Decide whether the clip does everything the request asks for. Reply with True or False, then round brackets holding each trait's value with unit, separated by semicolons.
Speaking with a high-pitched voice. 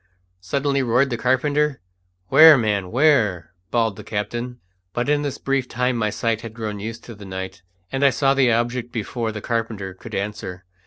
False (120 Hz)